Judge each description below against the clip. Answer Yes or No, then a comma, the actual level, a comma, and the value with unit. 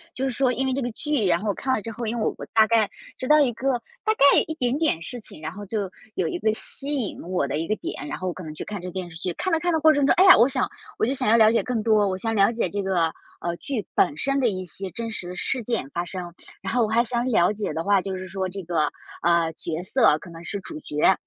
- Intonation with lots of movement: Yes, wide, 5.7 semitones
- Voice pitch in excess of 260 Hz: No, high, 215 Hz